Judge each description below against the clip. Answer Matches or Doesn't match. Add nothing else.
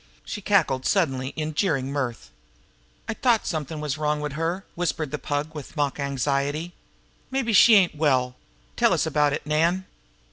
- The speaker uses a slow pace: Doesn't match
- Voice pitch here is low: Doesn't match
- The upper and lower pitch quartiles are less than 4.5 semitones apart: Matches